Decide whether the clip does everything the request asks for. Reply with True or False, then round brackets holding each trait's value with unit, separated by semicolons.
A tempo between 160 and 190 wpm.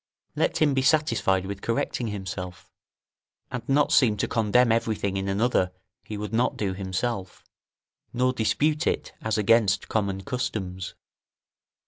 False (135 wpm)